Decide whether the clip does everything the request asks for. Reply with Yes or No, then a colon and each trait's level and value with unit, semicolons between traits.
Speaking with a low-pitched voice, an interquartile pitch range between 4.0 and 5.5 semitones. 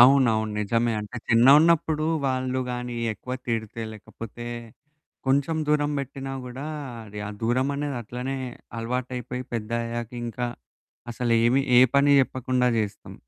No: low, 125 Hz; narrow, 2.6 semitones